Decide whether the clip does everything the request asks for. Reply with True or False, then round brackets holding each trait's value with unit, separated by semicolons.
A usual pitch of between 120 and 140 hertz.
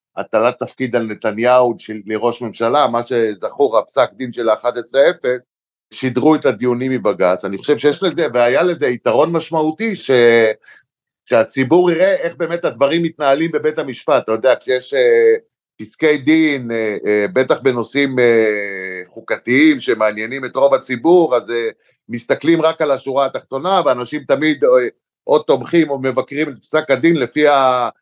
True (135 Hz)